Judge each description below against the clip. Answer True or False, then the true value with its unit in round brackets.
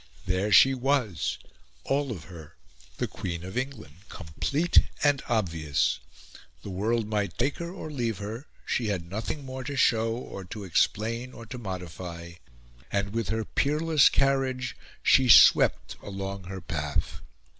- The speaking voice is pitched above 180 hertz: False (110 Hz)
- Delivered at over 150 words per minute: False (145 wpm)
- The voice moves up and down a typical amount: False (6.0 semitones)